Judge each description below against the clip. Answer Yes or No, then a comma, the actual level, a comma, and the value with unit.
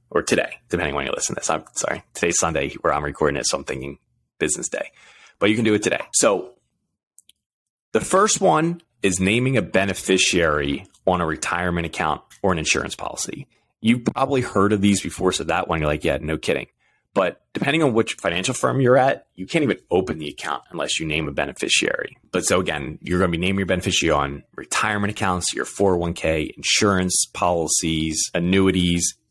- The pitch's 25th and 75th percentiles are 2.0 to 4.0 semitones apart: No, average, 4.7 semitones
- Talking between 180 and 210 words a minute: Yes, average, 195 wpm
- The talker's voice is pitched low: Yes, very low, 95 Hz